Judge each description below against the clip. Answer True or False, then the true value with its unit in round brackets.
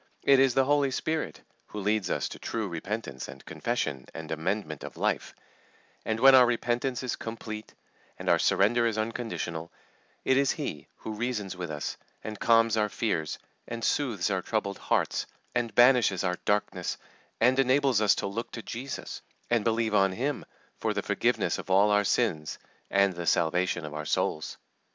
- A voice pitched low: True (110 Hz)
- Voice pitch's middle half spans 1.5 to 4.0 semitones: False (4.5 semitones)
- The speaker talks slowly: False (175 wpm)